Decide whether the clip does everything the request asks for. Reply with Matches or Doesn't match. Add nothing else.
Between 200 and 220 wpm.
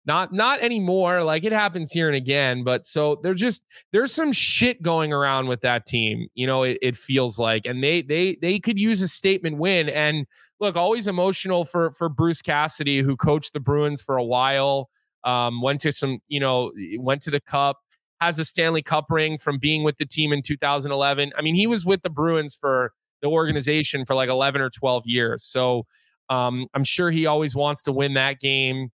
Matches